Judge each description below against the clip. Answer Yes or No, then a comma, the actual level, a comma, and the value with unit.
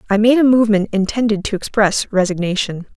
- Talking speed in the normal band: Yes, average, 160 wpm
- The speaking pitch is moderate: No, high, 210 Hz